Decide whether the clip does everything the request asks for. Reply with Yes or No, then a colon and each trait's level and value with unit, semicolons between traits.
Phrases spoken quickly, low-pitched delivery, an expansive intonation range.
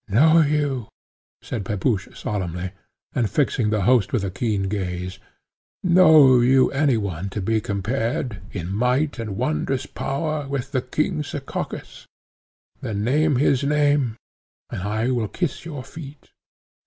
No: average, 140 wpm; low, 125 Hz; wide, 5.7 semitones